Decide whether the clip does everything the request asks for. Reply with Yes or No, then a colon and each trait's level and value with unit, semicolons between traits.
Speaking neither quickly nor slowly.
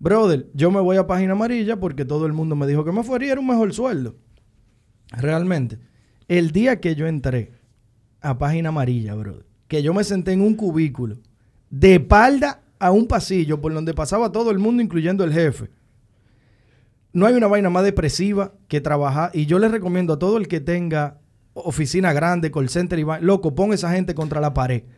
No: fast, 195 wpm